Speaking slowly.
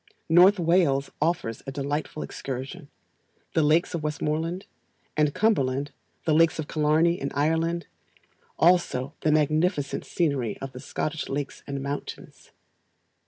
Yes: slow, 125 wpm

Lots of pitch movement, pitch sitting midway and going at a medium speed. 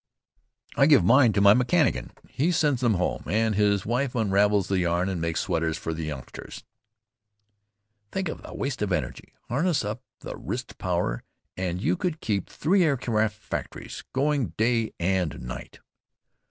No: wide, 6.4 semitones; low, 105 Hz; average, 155 wpm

